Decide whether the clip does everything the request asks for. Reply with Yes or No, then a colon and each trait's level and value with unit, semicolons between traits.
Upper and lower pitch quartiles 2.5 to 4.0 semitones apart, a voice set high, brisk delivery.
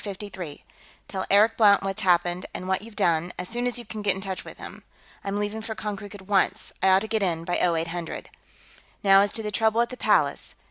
Yes: average, 2.9 semitones; high, 200 Hz; fast, 225 wpm